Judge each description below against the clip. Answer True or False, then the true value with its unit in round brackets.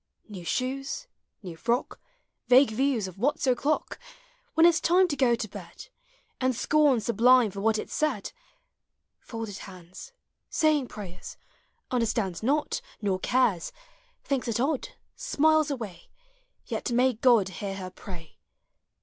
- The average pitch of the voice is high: True (240 Hz)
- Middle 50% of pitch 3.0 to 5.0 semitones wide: False (5.6 semitones)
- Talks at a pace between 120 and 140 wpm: True (135 wpm)